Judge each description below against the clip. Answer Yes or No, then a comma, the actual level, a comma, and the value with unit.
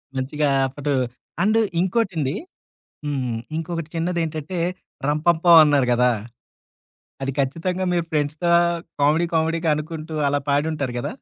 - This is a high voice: No, medium, 155 Hz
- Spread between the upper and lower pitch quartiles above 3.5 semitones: No, average, 2.7 semitones